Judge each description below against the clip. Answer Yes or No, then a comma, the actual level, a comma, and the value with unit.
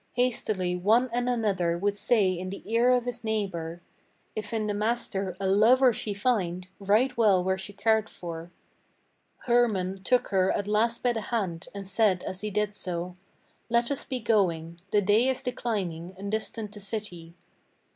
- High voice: Yes, high, 205 Hz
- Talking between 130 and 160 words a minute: No, average, 175 wpm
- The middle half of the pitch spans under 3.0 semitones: No, average, 3.8 semitones